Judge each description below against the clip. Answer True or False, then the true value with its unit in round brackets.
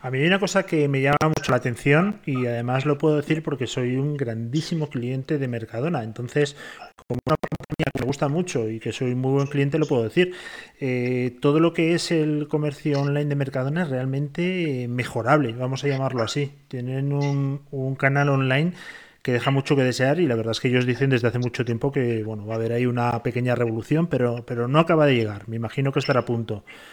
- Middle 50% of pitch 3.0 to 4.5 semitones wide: True (3.3 semitones)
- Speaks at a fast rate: True (220 wpm)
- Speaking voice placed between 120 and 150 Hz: True (135 Hz)